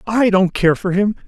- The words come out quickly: Yes, fast, 235 wpm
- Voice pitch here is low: No, high, 195 Hz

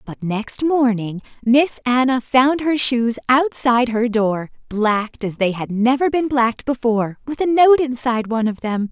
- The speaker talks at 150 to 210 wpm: Yes, average, 175 wpm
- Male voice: No, female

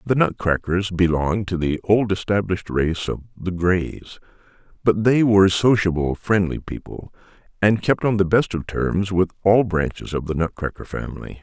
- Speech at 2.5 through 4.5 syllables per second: No, 4.9 syllables/s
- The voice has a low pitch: Yes, very low, 95 Hz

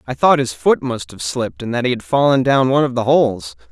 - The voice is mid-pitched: No, low, 125 Hz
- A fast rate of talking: Yes, fast, 275 wpm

